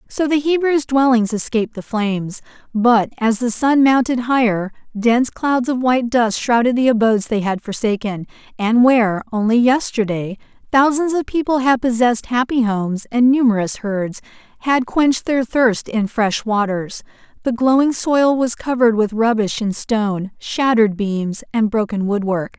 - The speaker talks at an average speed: Yes, average, 155 wpm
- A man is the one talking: No, female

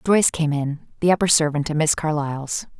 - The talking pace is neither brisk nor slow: Yes, average, 170 wpm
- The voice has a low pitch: No, medium, 155 Hz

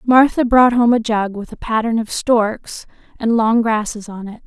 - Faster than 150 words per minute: Yes, average, 200 wpm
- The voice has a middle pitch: No, high, 225 Hz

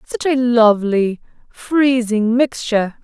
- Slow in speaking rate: Yes, slow, 100 wpm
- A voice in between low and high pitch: No, high, 240 Hz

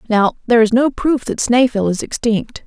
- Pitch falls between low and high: No, high, 235 Hz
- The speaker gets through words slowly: No, average, 200 wpm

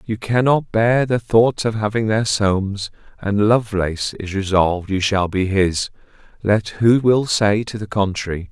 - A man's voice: Yes, male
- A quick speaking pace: No, average, 170 wpm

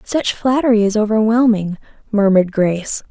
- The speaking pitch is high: Yes, high, 215 Hz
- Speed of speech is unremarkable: No, slow, 115 wpm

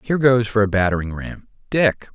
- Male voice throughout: Yes, male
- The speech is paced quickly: No, average, 195 wpm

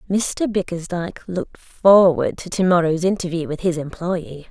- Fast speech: No, slow, 135 wpm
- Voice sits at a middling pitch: Yes, medium, 175 Hz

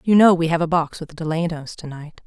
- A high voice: No, medium, 165 Hz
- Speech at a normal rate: No, fast, 265 wpm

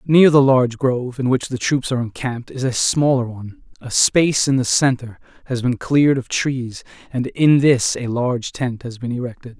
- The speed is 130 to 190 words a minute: No, fast, 205 wpm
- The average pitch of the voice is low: Yes, low, 130 Hz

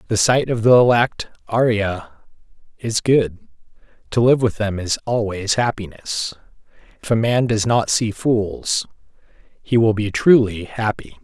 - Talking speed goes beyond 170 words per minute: No, average, 145 wpm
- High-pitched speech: No, low, 110 Hz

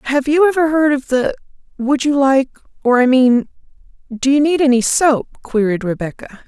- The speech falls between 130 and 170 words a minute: Yes, average, 160 wpm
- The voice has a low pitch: No, very high, 265 Hz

